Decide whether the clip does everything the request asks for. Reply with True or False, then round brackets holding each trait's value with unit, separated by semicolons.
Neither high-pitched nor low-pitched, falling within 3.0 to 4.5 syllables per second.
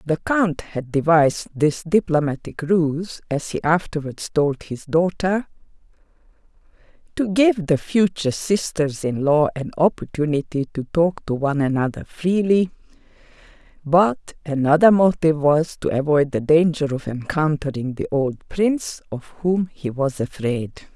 True (160 Hz; 4.0 syllables/s)